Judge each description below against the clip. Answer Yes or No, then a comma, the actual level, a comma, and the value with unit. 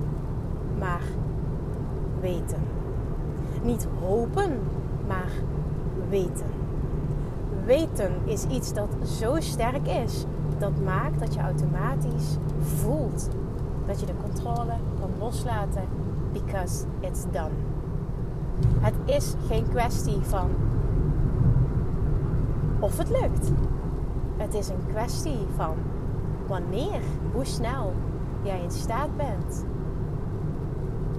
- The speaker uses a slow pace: Yes, slow, 90 wpm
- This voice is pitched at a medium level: Yes, medium, 145 Hz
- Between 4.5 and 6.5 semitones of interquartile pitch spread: No, narrow, 2.4 semitones